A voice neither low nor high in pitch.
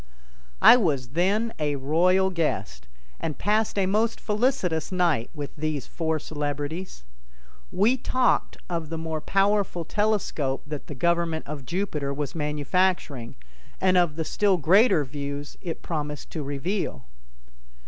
Yes: medium, 165 Hz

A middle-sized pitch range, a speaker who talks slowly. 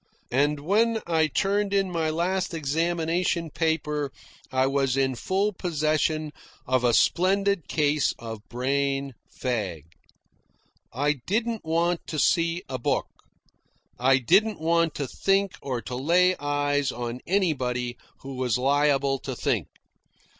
Yes: average, 4.5 semitones; slow, 130 wpm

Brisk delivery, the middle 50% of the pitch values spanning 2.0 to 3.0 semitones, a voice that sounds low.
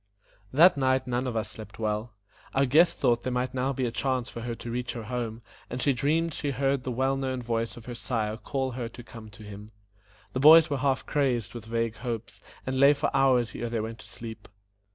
Yes: fast, 230 wpm; narrow, 2.6 semitones; low, 125 Hz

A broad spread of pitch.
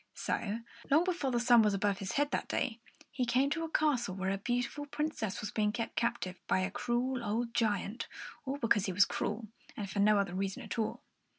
No: average, 4.2 semitones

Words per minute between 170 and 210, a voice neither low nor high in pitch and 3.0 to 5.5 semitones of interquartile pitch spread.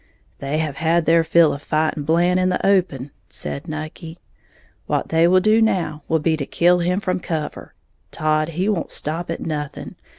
No: average, 185 wpm; medium, 165 Hz; narrow, 2.6 semitones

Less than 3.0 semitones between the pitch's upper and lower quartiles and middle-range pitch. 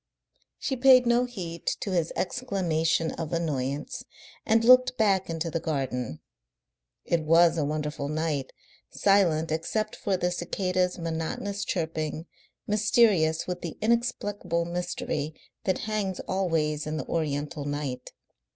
No: average, 4.4 semitones; medium, 170 Hz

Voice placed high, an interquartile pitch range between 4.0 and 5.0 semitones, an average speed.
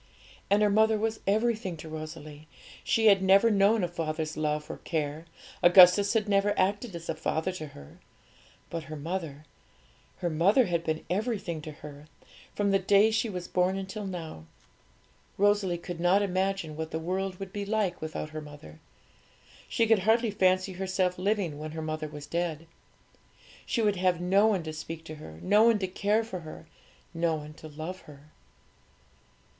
No: medium, 180 Hz; average, 4.3 semitones; average, 175 wpm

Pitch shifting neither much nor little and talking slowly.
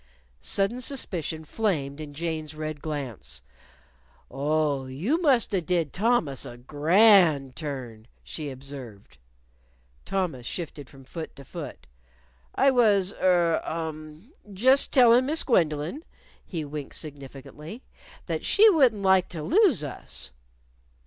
No: wide, 6.2 semitones; slow, 115 wpm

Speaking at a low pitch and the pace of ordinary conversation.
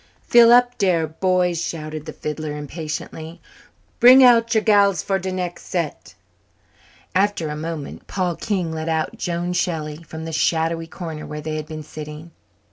No: medium, 165 Hz; average, 160 wpm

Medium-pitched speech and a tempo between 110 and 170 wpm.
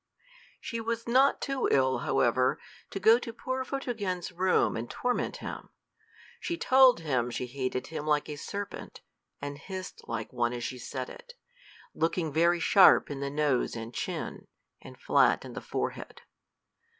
Yes: medium, 160 Hz; average, 160 wpm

